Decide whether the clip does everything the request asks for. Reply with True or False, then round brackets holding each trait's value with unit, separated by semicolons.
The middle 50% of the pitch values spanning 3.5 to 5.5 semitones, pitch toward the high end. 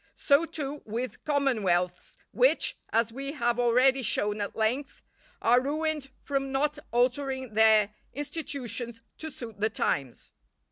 True (4.3 semitones; 255 Hz)